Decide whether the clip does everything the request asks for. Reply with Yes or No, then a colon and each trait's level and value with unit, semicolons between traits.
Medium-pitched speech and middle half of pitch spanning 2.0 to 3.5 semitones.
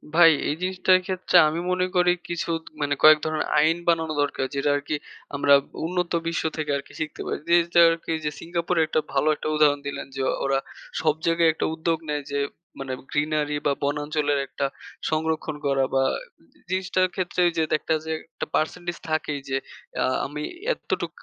Yes: medium, 155 Hz; average, 2.7 semitones